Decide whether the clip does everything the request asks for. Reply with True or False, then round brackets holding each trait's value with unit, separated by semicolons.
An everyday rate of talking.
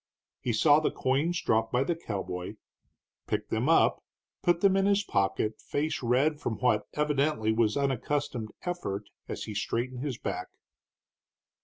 True (150 wpm)